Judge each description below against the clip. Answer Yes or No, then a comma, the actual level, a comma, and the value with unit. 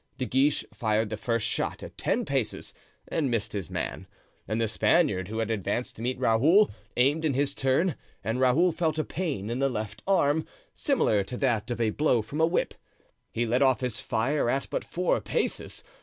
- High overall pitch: No, low, 125 Hz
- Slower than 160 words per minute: No, average, 200 wpm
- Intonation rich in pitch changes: No, average, 5.0 semitones